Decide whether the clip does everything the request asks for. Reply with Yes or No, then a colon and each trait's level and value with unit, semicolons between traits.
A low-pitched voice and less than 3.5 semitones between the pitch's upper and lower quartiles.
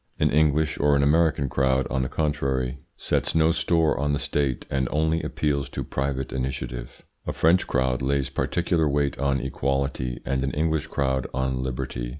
Yes: very low, 70 Hz; narrow, 2.4 semitones